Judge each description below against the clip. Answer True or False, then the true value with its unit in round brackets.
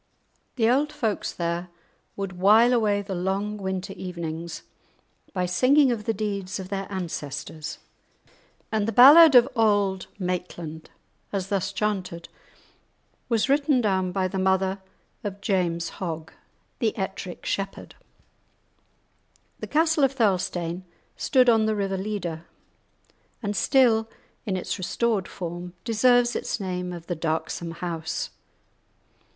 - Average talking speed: False (125 wpm)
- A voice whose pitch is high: True (195 Hz)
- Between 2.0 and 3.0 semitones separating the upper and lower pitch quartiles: False (3.8 semitones)